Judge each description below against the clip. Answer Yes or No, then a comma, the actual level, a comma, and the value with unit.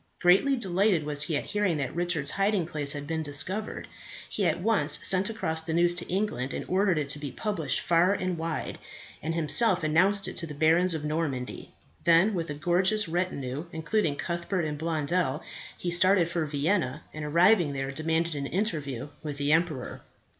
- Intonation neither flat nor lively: Yes, average, 3.7 semitones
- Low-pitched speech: No, medium, 165 Hz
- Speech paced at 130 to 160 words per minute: No, average, 180 wpm